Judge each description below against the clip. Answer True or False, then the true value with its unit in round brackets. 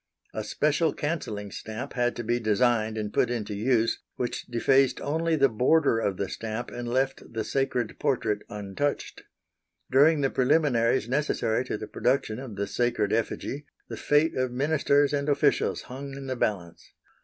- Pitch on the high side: False (125 Hz)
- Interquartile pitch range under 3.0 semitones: False (4.2 semitones)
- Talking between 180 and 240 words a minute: False (165 wpm)